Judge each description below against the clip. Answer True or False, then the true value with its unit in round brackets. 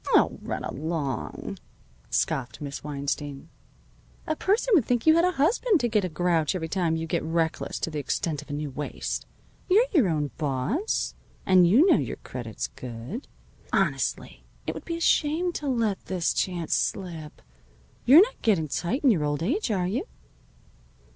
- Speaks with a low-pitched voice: False (180 Hz)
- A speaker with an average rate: True (175 wpm)